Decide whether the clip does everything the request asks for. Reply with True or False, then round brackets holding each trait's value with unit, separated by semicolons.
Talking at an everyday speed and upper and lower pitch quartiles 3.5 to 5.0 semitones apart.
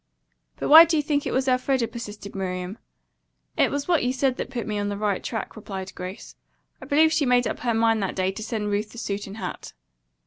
False (235 wpm; 4.4 semitones)